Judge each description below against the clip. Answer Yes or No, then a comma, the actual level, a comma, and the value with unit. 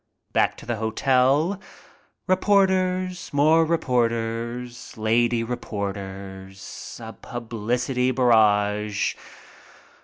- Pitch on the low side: Yes, low, 120 Hz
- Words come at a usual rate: No, slow, 70 wpm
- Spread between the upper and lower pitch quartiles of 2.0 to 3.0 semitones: No, average, 4.7 semitones